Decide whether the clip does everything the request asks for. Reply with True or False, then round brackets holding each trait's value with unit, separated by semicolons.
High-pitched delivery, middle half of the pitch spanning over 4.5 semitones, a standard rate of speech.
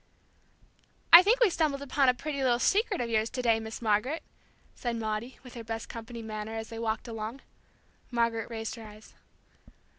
False (230 Hz; 3.0 semitones; 180 wpm)